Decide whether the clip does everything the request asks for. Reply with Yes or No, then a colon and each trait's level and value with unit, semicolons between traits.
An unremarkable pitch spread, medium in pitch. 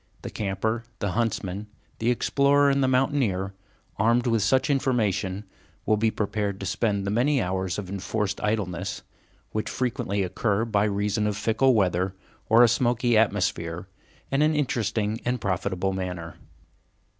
No: average, 3.7 semitones; low, 105 Hz